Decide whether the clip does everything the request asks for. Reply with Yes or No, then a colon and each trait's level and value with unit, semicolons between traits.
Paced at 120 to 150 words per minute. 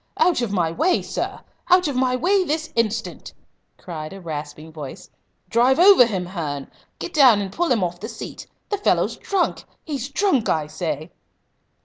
No: average, 170 wpm